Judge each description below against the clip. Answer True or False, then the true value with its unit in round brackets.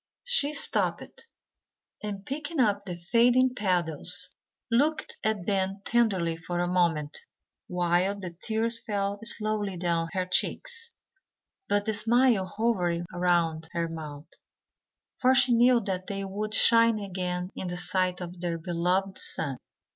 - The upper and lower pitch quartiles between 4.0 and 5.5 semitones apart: True (4.6 semitones)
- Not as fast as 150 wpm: True (135 wpm)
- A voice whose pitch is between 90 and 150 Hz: False (195 Hz)